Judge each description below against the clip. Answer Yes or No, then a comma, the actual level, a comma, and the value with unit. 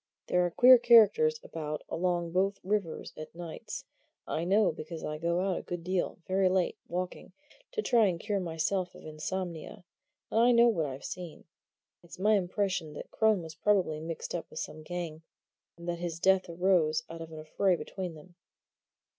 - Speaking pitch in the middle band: Yes, medium, 175 Hz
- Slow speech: No, average, 180 wpm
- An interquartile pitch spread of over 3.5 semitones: No, average, 3.1 semitones